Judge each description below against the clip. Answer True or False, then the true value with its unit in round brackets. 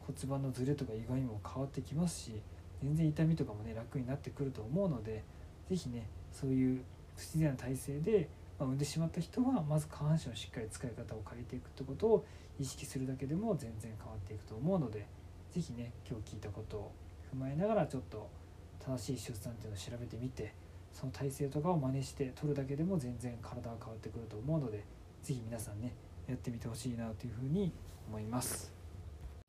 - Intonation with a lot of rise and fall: False (4.7 semitones)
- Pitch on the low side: True (125 Hz)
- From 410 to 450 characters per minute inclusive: True (415 characters per minute)